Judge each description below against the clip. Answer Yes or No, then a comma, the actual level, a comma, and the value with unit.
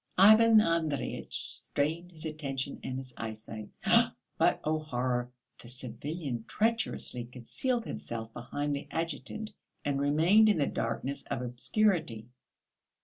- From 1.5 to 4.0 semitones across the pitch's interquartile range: No, wide, 5.5 semitones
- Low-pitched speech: No, medium, 145 Hz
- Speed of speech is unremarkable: No, slow, 120 wpm